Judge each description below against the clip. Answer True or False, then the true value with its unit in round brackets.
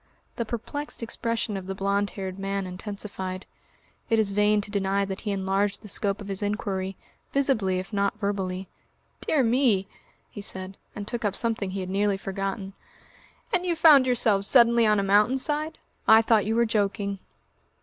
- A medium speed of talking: True (175 wpm)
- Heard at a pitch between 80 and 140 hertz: False (205 Hz)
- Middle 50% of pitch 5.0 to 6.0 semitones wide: False (2.7 semitones)